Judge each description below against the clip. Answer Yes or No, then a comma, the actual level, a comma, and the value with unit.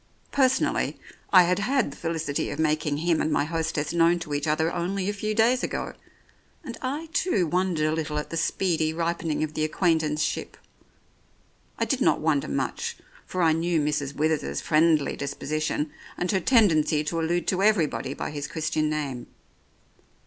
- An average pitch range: Yes, average, 3.1 semitones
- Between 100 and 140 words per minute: No, average, 170 wpm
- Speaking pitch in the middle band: Yes, medium, 160 Hz